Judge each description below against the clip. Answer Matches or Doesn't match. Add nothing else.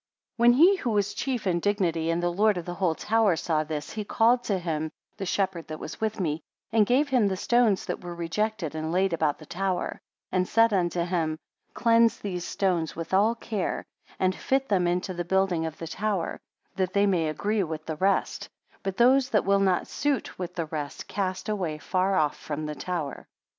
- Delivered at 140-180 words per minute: Doesn't match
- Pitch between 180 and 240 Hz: Matches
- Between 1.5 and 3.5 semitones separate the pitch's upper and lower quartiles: Doesn't match